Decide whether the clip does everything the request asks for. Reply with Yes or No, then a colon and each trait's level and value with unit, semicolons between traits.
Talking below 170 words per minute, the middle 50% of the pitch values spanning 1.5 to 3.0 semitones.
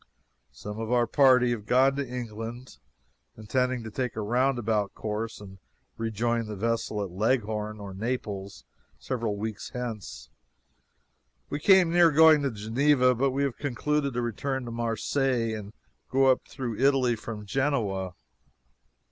No: average, 140 wpm; average, 3.6 semitones